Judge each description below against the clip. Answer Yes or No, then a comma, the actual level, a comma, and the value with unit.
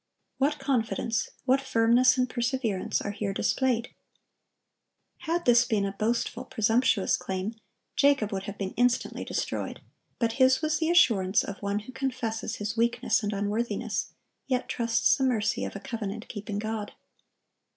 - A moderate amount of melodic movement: Yes, average, 3.8 semitones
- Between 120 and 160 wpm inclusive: Yes, average, 150 wpm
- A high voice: Yes, high, 230 Hz